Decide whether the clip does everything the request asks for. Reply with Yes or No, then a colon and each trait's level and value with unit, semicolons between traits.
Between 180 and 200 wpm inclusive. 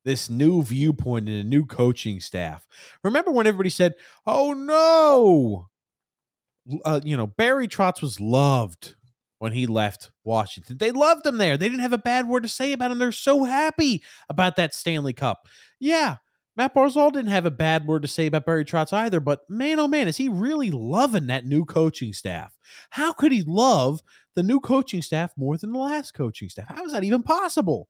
Yes: average, 195 wpm